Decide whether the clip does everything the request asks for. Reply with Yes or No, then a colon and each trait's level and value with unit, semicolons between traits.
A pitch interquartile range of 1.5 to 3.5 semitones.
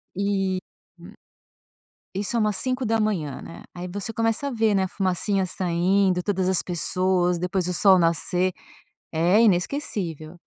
Yes: average, 2.7 semitones